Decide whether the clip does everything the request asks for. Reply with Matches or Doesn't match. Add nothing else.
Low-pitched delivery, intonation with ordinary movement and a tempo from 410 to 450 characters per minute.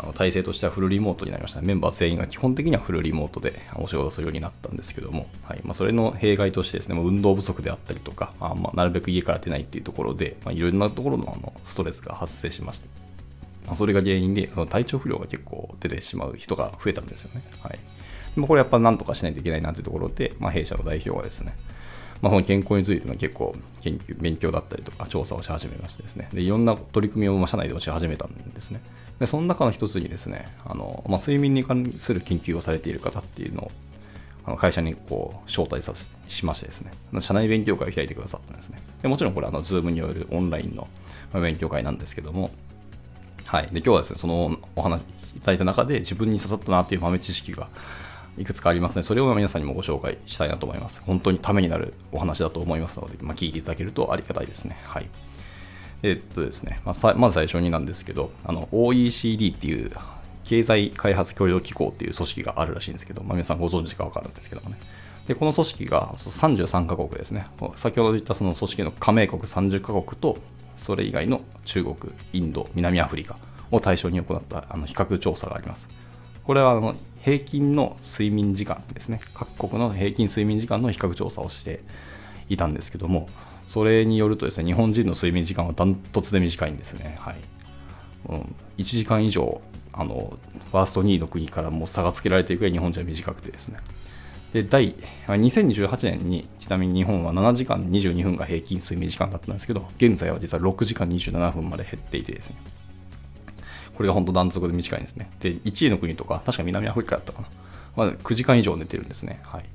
Matches